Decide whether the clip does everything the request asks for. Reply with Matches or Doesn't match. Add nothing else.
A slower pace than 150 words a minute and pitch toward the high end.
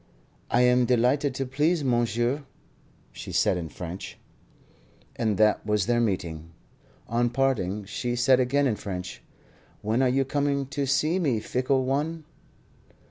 Doesn't match